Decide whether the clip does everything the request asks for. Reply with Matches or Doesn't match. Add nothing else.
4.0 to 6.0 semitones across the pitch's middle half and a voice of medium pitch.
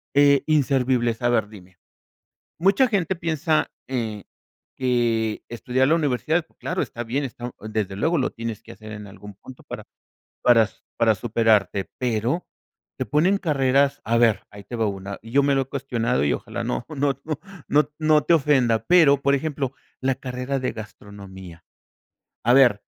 Doesn't match